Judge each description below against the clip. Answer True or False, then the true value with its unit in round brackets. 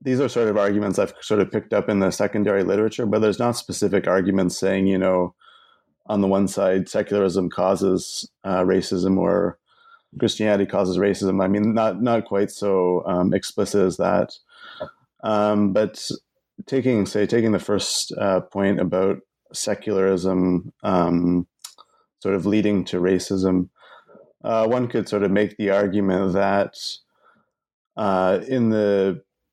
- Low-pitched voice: True (100 Hz)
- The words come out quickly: False (150 wpm)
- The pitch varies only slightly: True (1.9 semitones)